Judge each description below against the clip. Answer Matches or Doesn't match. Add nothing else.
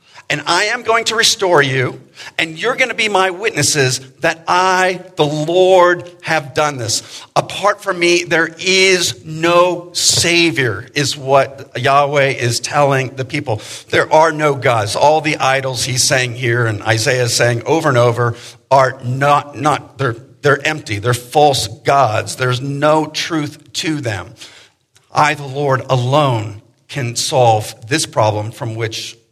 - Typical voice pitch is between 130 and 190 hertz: Matches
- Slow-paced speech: Doesn't match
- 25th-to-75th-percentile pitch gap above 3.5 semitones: Matches